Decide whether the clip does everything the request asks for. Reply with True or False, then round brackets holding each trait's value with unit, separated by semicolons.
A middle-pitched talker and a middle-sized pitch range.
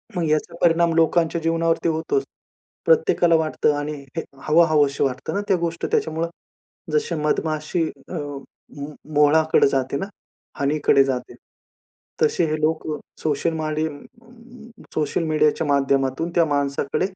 False (155 Hz; 2.2 semitones)